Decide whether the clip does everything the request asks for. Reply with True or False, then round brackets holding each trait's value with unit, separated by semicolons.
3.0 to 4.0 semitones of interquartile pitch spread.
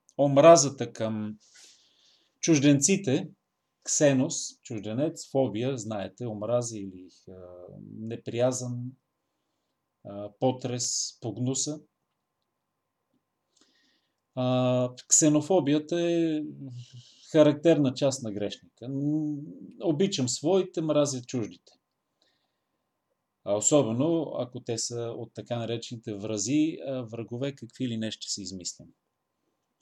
False (4.7 semitones)